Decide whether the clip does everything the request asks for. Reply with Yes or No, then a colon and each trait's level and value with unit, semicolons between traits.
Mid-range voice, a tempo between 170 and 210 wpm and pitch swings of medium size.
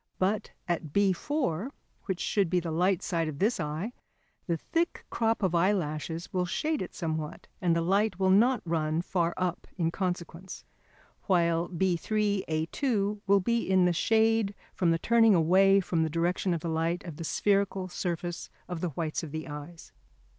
Yes: medium, 180 Hz; average, 175 wpm; average, 3.2 semitones